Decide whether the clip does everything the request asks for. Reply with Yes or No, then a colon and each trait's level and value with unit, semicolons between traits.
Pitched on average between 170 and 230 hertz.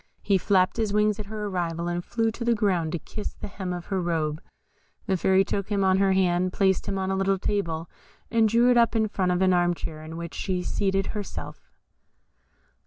Yes: high, 190 Hz